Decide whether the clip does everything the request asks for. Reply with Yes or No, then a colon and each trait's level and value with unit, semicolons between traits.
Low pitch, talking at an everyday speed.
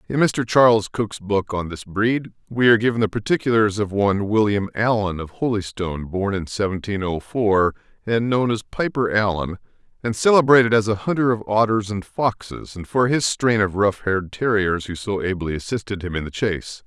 Yes: low, 105 Hz; average, 190 wpm